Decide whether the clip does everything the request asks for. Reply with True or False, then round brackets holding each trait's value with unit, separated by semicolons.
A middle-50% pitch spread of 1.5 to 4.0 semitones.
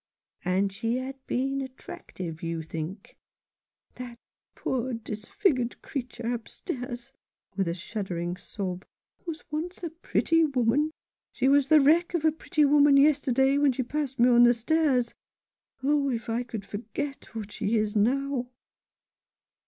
False (4.5 semitones)